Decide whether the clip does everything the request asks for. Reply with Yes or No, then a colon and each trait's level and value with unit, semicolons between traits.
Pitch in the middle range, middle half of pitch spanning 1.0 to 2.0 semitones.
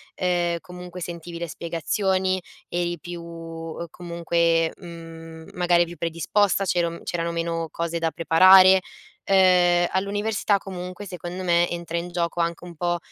Yes: medium, 175 Hz; narrow, 1.3 semitones